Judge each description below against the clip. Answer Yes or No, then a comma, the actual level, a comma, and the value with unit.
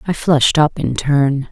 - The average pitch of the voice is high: No, medium, 145 Hz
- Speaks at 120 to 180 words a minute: No, average, 200 wpm